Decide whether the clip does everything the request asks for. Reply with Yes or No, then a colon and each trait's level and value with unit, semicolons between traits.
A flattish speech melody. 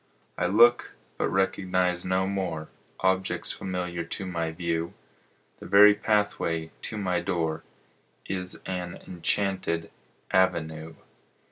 Yes: narrow, 2.3 semitones